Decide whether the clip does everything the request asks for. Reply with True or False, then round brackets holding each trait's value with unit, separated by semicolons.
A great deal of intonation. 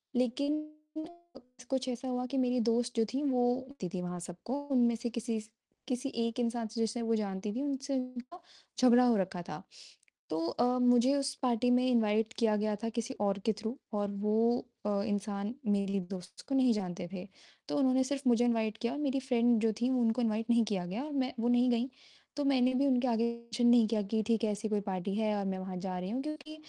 False (3.2 semitones)